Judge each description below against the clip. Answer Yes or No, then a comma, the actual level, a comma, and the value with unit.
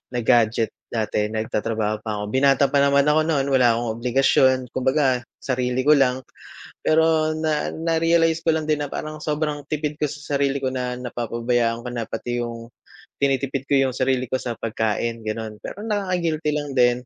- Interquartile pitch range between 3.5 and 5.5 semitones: Yes, average, 4.2 semitones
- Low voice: Yes, low, 130 Hz